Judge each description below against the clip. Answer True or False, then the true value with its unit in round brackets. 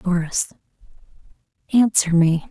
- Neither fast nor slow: False (70 wpm)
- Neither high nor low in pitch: True (180 Hz)